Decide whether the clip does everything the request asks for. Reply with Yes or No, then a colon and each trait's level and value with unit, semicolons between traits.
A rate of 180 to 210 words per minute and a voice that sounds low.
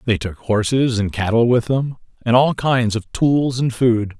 Yes: average, 200 wpm; low, 120 Hz